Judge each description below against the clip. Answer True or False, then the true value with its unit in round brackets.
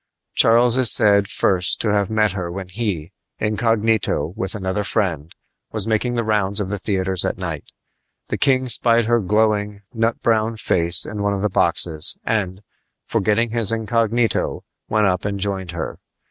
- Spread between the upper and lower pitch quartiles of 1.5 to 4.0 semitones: True (3.0 semitones)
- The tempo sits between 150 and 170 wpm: True (165 wpm)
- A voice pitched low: True (105 Hz)